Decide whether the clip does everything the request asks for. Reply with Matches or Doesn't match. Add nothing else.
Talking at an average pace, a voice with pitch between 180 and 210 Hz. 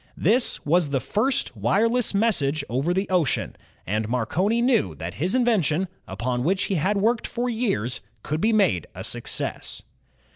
Matches